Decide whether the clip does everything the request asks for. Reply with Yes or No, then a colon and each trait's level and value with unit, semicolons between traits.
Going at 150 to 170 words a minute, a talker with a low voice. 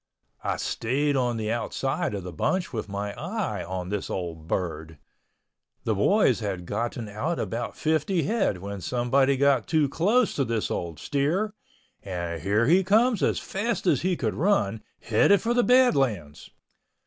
Yes: average, 160 wpm; low, 120 Hz